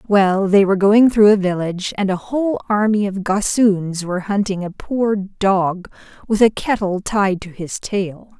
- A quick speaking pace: No, average, 180 wpm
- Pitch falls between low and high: No, high, 200 Hz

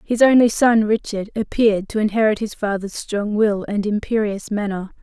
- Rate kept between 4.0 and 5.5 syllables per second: Yes, 5.0 syllables/s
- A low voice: No, high, 210 Hz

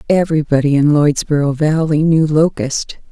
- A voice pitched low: No, medium, 150 Hz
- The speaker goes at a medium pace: No, slow, 115 wpm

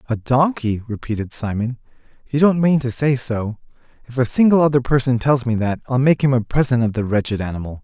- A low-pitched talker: Yes, low, 125 Hz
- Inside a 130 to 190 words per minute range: No, fast, 205 wpm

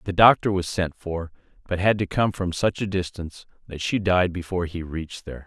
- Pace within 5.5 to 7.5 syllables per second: Yes, 5.7 syllables/s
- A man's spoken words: Yes, male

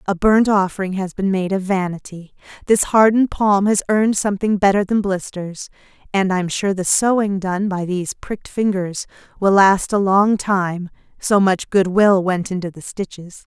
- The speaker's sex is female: Yes, female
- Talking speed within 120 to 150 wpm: No, average, 175 wpm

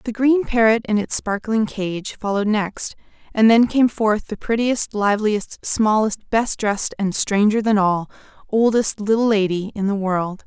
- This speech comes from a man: No, female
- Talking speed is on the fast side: No, average, 165 wpm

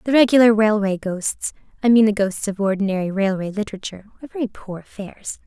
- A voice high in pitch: Yes, high, 210 Hz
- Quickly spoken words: No, average, 155 wpm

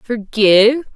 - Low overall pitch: No, high, 230 Hz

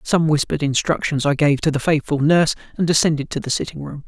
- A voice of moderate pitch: Yes, medium, 150 Hz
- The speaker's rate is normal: No, fast, 220 wpm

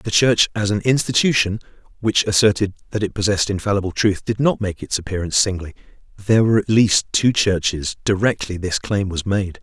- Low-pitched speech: Yes, low, 100 Hz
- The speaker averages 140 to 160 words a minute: No, average, 180 wpm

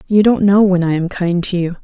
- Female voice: Yes, female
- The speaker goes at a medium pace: No, fast, 295 wpm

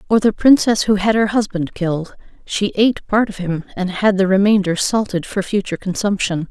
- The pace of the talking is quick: No, average, 195 wpm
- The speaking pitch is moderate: No, high, 200 Hz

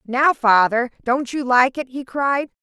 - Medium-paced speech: Yes, average, 185 wpm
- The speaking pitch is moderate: No, very high, 260 Hz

